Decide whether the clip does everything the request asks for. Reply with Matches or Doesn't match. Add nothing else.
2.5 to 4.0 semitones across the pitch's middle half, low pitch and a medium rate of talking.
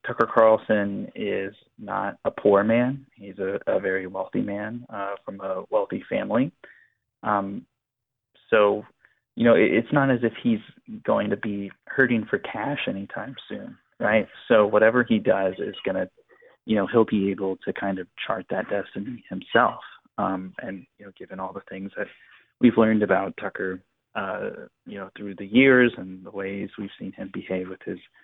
Matches